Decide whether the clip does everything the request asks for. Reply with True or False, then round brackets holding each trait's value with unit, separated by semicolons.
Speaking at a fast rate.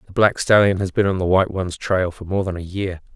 True (285 wpm)